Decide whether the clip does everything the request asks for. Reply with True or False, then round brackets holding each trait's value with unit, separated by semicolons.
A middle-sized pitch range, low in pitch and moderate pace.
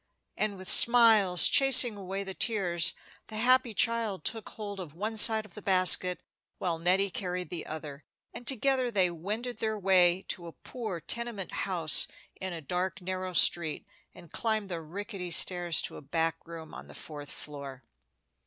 False (4.1 semitones; 185 Hz; 170 wpm)